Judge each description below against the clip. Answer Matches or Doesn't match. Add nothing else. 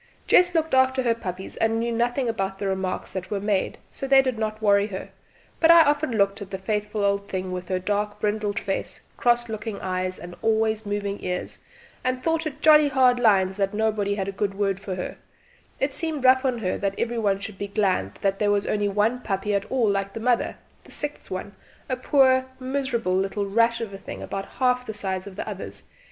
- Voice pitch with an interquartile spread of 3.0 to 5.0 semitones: Matches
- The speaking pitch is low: Doesn't match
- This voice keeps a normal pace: Doesn't match